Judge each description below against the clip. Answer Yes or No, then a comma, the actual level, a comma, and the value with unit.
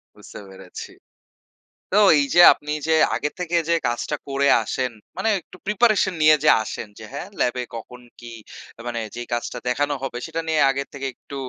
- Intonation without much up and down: No, average, 4.8 semitones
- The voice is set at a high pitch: No, medium, 140 Hz